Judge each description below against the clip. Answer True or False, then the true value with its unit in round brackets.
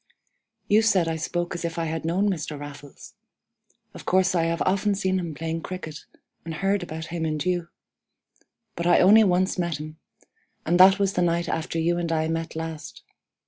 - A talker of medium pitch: True (170 Hz)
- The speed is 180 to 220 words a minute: True (190 wpm)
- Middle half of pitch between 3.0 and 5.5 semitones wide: False (2.4 semitones)